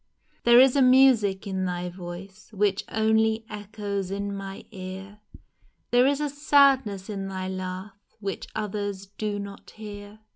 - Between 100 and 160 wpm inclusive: Yes, average, 145 wpm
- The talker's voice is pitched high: Yes, high, 205 Hz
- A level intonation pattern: Yes, narrow, 2.3 semitones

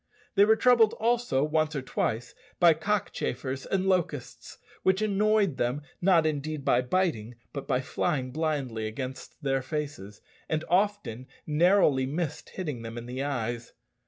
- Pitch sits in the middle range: Yes, medium, 150 Hz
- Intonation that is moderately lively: No, wide, 6.4 semitones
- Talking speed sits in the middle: Yes, average, 145 wpm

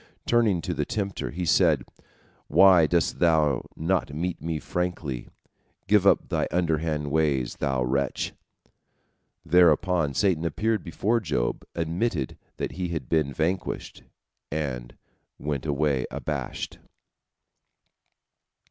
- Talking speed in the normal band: No, slow, 110 wpm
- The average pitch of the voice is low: Yes, very low, 80 Hz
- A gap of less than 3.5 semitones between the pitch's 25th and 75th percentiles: No, average, 3.8 semitones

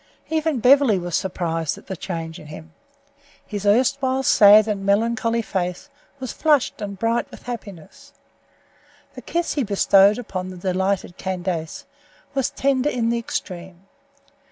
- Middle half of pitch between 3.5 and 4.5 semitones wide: No, average, 5.1 semitones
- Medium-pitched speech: No, high, 205 Hz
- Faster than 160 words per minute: No, average, 140 wpm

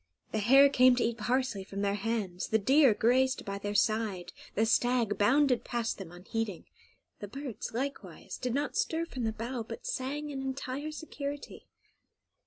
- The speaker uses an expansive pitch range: No, average, 4.5 semitones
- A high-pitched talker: Yes, high, 240 Hz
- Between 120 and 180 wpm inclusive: Yes, average, 170 wpm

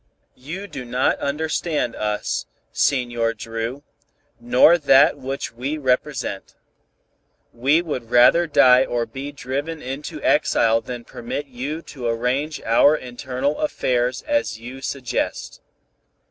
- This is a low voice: Yes, low, 130 Hz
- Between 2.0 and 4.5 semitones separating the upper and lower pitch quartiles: Yes, average, 3.3 semitones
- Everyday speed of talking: No, slow, 120 wpm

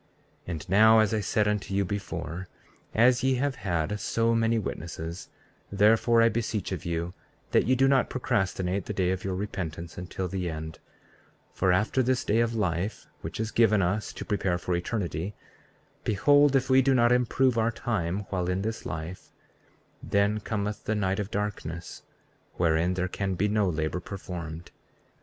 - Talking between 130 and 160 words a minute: No, average, 175 wpm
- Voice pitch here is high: No, low, 100 Hz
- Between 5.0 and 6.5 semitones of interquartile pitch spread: No, average, 4.1 semitones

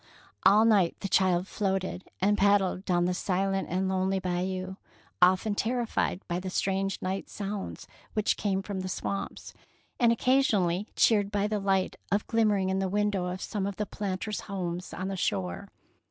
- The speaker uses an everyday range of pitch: No, narrow, 1.8 semitones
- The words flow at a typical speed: Yes, average, 170 wpm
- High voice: Yes, high, 195 Hz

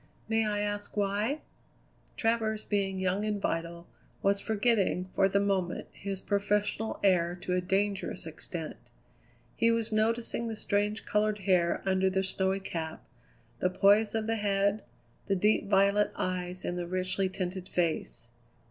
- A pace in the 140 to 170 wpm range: Yes, average, 150 wpm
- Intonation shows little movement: Yes, narrow, 2.3 semitones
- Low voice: No, high, 200 Hz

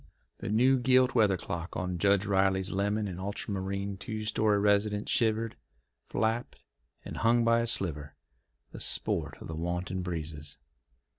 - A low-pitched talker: Yes, low, 100 Hz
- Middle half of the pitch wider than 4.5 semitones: No, average, 3.2 semitones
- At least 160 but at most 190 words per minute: No, average, 145 wpm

